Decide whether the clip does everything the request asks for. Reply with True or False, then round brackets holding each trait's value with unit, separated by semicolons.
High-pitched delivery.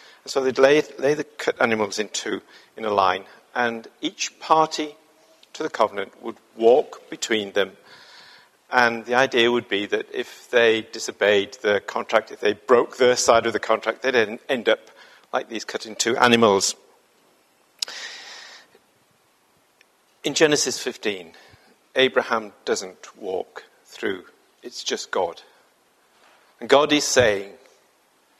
False (135 Hz)